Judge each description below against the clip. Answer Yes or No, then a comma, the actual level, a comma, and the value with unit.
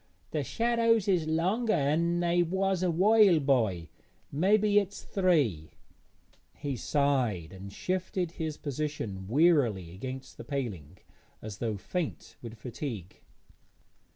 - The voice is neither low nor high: Yes, medium, 150 Hz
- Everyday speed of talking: No, slow, 120 wpm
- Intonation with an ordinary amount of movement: No, wide, 8.4 semitones